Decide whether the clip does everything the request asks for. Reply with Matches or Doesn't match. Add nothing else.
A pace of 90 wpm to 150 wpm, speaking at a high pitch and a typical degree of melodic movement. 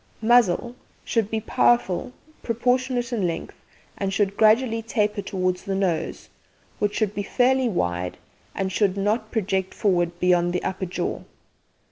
Matches